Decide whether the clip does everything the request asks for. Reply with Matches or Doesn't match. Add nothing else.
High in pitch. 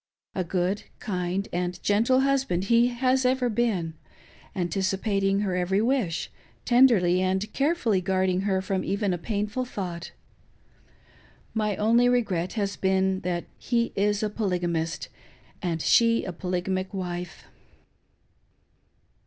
Matches